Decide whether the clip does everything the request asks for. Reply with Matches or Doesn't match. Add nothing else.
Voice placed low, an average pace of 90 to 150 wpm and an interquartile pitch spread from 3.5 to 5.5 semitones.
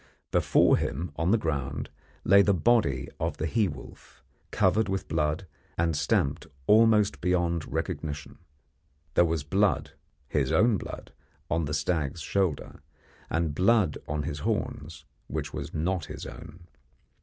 Matches